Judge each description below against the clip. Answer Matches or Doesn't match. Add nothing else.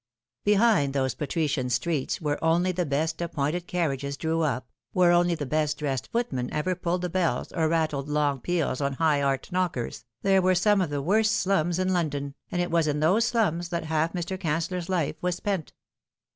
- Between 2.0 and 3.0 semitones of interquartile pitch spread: Doesn't match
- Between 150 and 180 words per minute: Doesn't match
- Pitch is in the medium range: Matches